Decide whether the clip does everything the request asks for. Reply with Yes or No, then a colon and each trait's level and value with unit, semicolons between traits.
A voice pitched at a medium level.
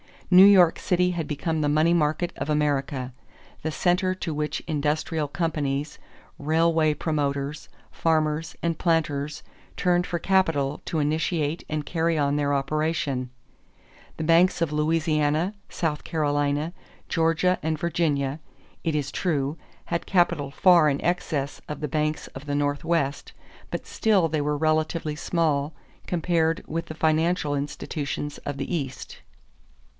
Yes: medium, 155 Hz